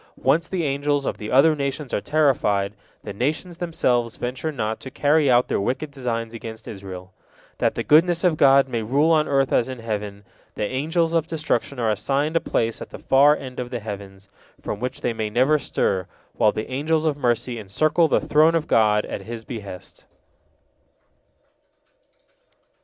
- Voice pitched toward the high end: No, low, 130 Hz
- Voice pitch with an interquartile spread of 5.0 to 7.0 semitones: Yes, average, 5.3 semitones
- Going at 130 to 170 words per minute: No, average, 180 wpm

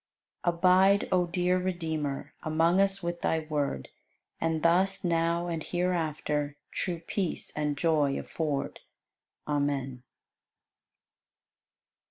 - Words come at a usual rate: No, slow, 105 wpm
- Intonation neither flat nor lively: Yes, average, 3.1 semitones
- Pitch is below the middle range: No, medium, 165 Hz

